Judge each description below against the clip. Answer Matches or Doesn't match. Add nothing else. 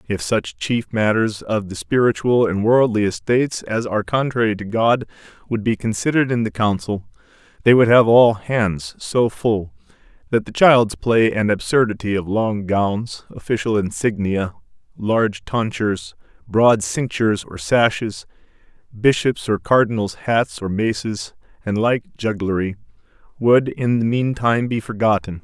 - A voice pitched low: Matches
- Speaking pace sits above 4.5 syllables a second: Doesn't match